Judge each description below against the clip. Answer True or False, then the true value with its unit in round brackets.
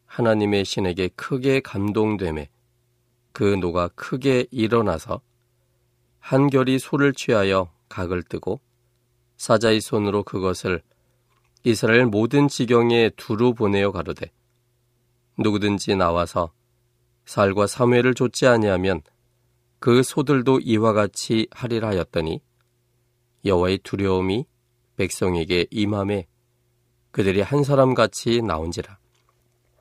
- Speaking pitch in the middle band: False (120 Hz)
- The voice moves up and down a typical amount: True (3.4 semitones)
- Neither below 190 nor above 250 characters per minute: True (240 characters per minute)